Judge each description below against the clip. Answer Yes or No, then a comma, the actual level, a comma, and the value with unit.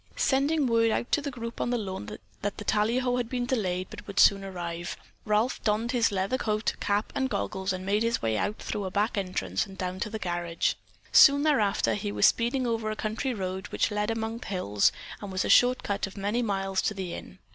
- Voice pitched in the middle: No, high, 210 Hz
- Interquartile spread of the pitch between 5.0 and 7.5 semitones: No, average, 3.7 semitones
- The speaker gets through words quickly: Yes, fast, 225 wpm